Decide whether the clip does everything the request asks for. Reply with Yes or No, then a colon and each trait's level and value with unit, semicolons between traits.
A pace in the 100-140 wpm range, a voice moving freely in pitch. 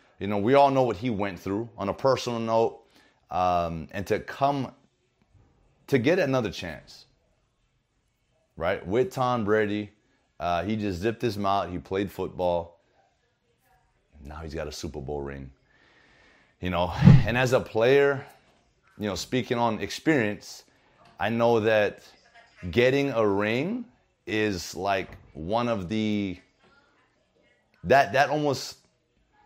Yes: slow, 135 wpm; wide, 5.7 semitones